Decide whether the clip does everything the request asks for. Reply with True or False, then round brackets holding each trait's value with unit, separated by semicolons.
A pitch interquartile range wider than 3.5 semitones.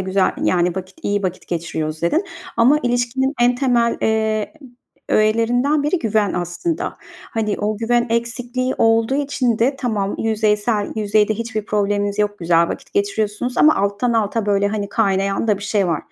False (3.0 semitones)